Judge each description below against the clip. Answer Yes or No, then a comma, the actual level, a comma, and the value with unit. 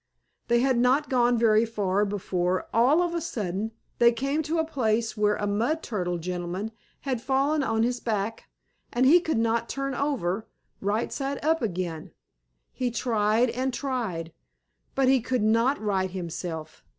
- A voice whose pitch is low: No, high, 230 Hz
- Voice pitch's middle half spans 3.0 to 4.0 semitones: No, average, 4.7 semitones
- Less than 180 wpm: Yes, average, 160 wpm